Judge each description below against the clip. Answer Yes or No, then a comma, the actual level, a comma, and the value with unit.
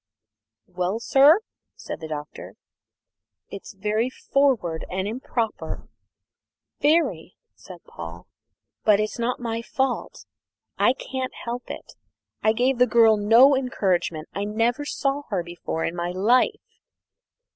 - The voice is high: Yes, high, 225 Hz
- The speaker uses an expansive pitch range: Yes, wide, 5.7 semitones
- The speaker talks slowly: Yes, slow, 125 wpm